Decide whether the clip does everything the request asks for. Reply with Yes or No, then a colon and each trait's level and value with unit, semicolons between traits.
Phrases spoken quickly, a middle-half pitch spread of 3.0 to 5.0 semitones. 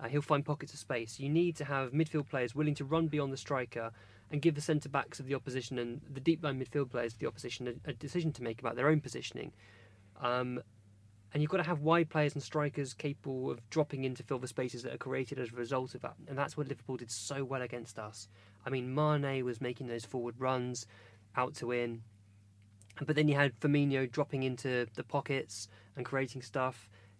Yes: fast, 225 wpm; average, 3.4 semitones